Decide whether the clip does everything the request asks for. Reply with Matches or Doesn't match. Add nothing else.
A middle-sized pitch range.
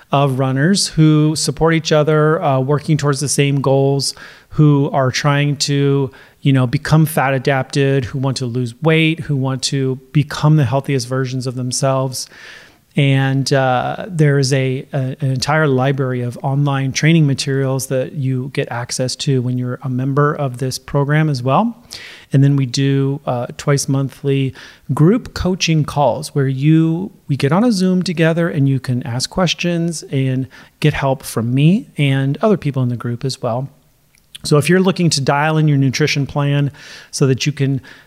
Doesn't match